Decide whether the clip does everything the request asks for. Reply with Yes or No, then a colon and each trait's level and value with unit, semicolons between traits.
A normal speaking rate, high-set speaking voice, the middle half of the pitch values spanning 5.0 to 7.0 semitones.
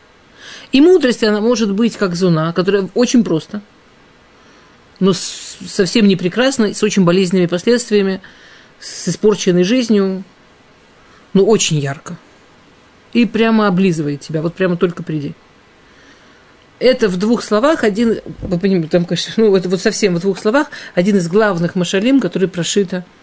No: average, 135 wpm; high, 195 Hz; average, 3.3 semitones